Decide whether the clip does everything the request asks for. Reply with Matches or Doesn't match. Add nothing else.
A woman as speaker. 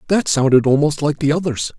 Doesn't match